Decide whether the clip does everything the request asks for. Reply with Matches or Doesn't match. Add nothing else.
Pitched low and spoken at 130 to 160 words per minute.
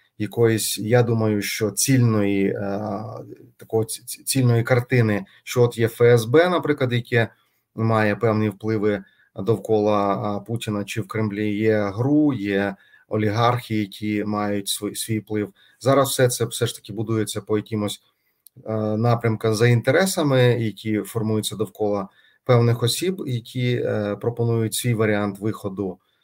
Doesn't match